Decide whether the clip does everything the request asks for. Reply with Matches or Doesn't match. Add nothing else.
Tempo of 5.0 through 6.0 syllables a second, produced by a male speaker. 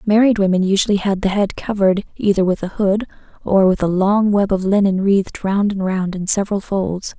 Doesn't match